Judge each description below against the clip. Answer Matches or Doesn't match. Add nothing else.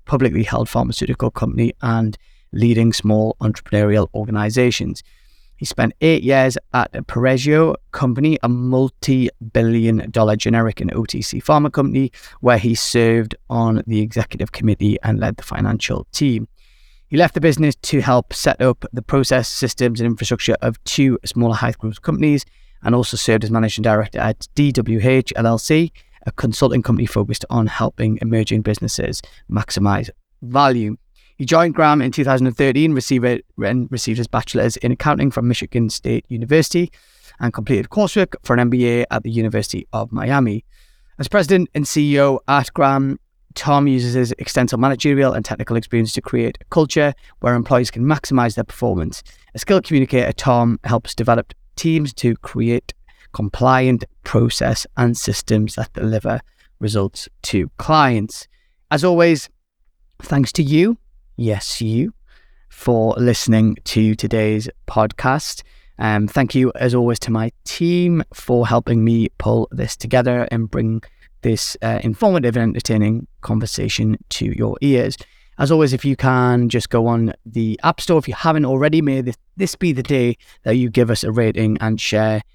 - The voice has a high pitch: Doesn't match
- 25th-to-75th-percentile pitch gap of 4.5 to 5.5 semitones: Doesn't match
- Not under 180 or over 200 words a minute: Doesn't match